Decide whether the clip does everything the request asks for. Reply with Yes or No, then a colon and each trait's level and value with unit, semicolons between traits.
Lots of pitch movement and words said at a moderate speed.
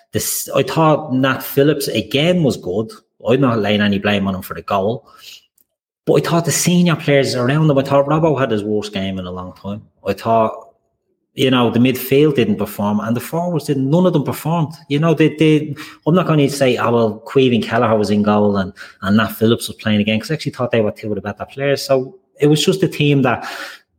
No: wide, 5.7 semitones; fast, 235 wpm